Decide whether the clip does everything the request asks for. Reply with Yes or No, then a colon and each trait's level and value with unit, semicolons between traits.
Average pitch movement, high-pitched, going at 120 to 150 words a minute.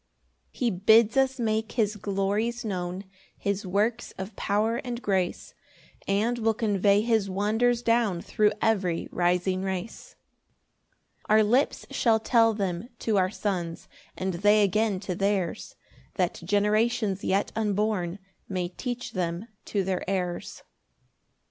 Yes: average, 3.0 semitones; high, 205 Hz; slow, 135 wpm